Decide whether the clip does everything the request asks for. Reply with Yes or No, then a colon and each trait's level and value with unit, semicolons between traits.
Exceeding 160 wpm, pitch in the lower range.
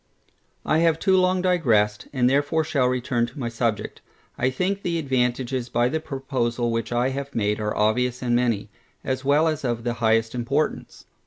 Yes: average, 180 wpm; low, 125 Hz